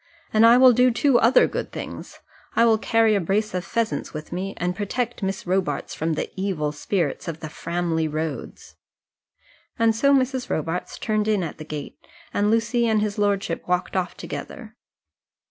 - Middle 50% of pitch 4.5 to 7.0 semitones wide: Yes, average, 5.1 semitones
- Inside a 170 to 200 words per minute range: Yes, average, 180 wpm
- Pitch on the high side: Yes, high, 200 Hz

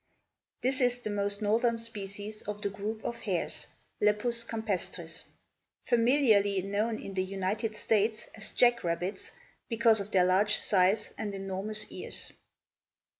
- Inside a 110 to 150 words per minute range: Yes, slow, 135 wpm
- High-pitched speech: Yes, high, 210 Hz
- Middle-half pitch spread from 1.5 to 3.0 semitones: Yes, narrow, 2.5 semitones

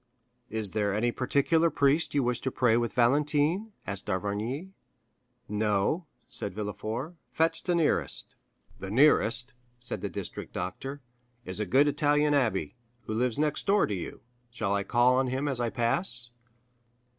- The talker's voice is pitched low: Yes, low, 125 Hz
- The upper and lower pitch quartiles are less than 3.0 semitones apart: No, average, 5.2 semitones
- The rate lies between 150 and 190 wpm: Yes, average, 155 wpm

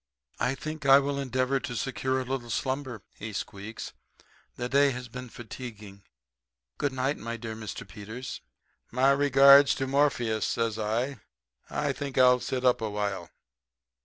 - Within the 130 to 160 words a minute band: Yes, average, 155 wpm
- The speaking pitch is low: Yes, low, 125 Hz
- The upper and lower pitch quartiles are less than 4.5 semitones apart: Yes, average, 3.4 semitones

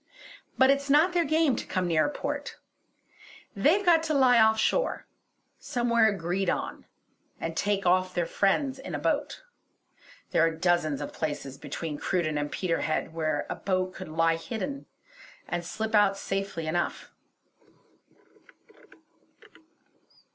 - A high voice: Yes, high, 195 Hz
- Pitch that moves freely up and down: Yes, wide, 8.1 semitones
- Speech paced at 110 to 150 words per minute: Yes, average, 140 wpm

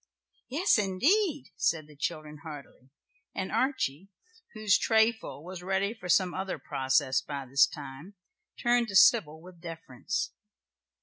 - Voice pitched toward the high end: No, medium, 180 Hz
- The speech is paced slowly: Yes, slow, 130 wpm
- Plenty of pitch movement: Yes, wide, 6.4 semitones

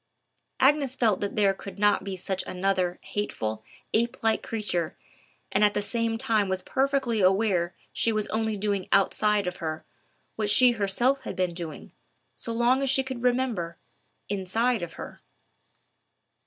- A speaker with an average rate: Yes, average, 155 wpm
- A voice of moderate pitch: No, high, 210 Hz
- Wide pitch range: No, average, 3.9 semitones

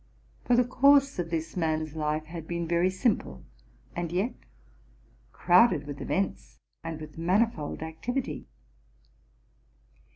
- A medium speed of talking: No, slow, 120 wpm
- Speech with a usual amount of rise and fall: Yes, average, 4.5 semitones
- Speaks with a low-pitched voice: No, medium, 170 Hz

